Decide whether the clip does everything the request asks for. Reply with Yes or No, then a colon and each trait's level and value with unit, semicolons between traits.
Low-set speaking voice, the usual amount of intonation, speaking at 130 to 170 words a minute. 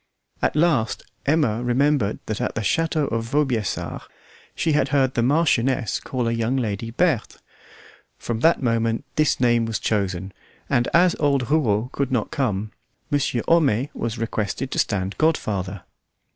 Yes: low, 120 Hz; average, 4.8 semitones; average, 150 wpm